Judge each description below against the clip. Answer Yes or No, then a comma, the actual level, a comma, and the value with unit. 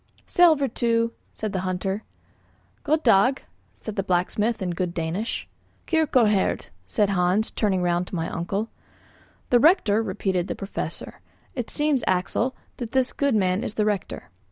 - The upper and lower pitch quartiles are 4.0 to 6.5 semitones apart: Yes, average, 4.6 semitones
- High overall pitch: Yes, high, 210 Hz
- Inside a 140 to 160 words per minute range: Yes, average, 145 wpm